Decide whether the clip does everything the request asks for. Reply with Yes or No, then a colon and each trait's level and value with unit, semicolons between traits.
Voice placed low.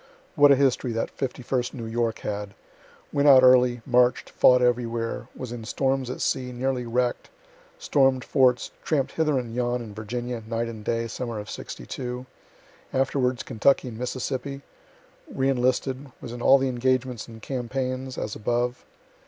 Yes: low, 125 Hz